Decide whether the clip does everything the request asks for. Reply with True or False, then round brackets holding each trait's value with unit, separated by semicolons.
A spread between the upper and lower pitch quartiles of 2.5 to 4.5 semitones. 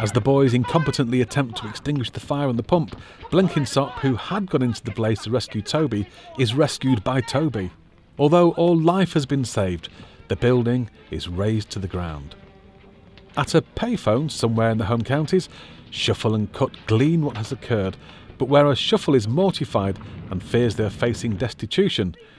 False (5.0 semitones)